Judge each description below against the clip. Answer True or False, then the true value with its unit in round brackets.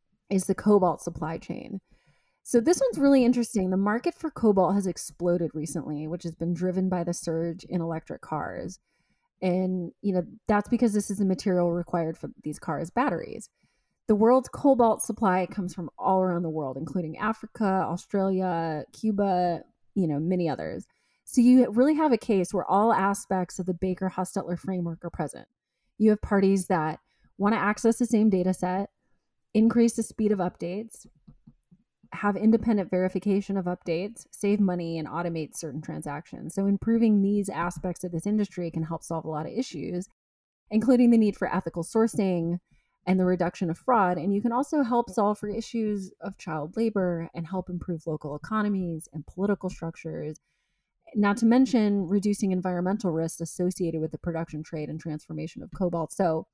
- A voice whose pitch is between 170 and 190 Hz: True (185 Hz)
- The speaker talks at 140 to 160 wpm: False (170 wpm)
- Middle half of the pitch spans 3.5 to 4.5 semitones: True (3.8 semitones)